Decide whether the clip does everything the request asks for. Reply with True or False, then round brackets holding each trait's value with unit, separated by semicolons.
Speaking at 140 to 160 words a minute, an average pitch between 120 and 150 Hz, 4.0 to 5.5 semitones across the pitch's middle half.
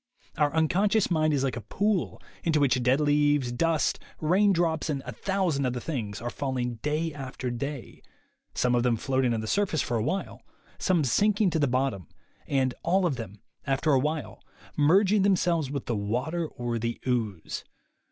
False (180 wpm; 140 Hz; 5.2 semitones)